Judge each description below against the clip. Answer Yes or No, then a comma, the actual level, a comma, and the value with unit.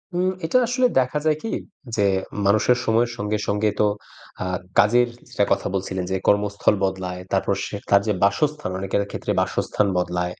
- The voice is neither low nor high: No, low, 105 Hz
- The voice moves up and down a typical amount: Yes, average, 4.0 semitones